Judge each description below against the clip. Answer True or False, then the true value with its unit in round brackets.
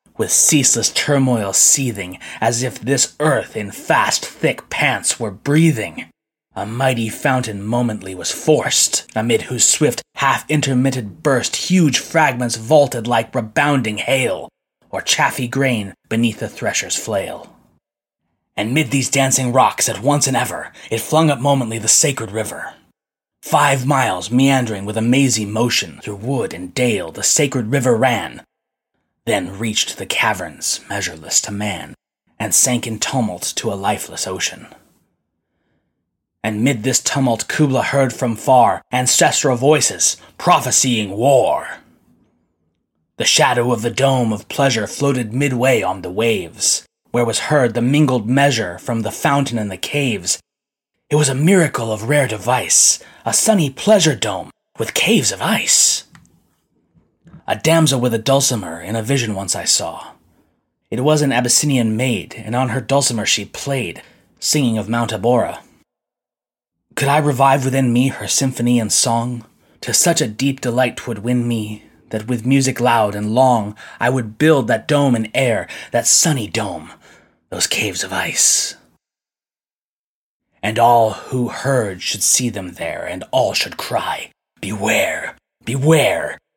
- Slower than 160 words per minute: True (145 wpm)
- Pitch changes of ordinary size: True (3.5 semitones)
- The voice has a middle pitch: False (125 Hz)